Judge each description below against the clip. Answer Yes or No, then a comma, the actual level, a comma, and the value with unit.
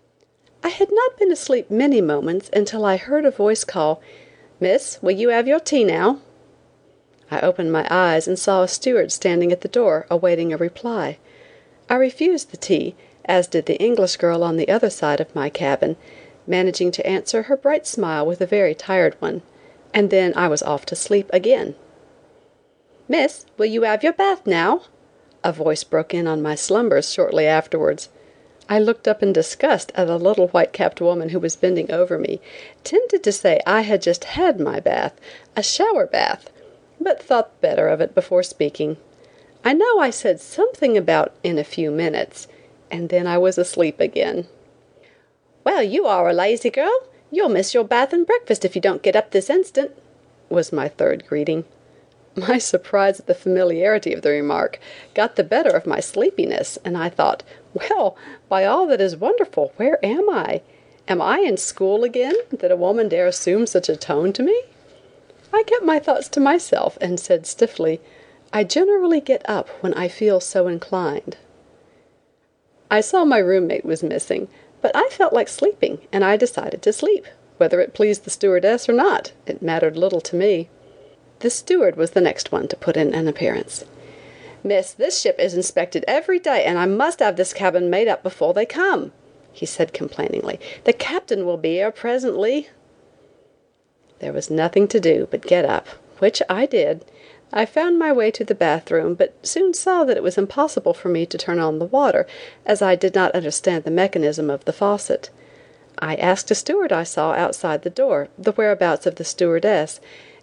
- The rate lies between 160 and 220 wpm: Yes, average, 185 wpm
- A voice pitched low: No, high, 210 Hz